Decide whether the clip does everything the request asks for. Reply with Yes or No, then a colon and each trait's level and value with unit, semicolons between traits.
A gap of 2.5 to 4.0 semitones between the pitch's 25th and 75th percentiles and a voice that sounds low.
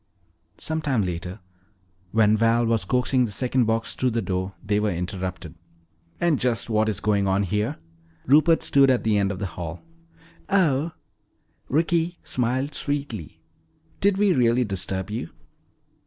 No: wide, 5.5 semitones; low, 115 Hz